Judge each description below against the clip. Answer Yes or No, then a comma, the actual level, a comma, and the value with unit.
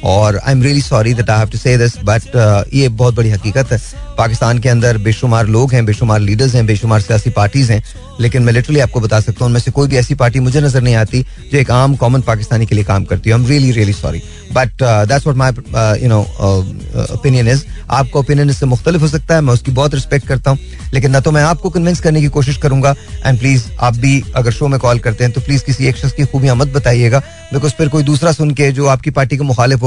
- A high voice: No, low, 125 Hz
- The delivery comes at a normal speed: No, fast, 235 wpm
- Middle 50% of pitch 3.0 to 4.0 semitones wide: Yes, average, 3.4 semitones